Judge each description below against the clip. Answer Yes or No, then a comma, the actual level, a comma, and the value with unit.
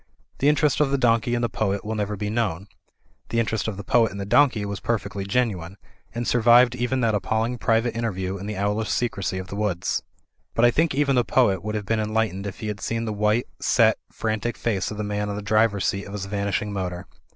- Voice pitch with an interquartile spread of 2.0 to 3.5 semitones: Yes, average, 2.8 semitones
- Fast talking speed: Yes, fast, 235 wpm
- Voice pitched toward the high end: No, low, 105 Hz